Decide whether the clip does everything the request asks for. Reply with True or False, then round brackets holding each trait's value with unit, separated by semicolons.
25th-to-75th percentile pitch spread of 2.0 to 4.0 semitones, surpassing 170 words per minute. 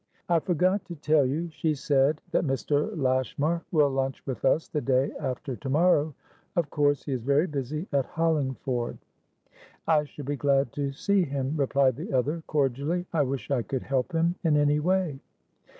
True (2.9 semitones; 180 wpm)